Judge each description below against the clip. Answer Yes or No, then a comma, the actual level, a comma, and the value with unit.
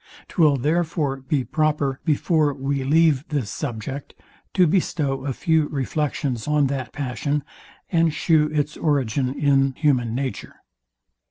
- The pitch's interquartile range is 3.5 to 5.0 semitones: No, narrow, 2.4 semitones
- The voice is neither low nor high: Yes, medium, 145 Hz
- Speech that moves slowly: Yes, slow, 125 wpm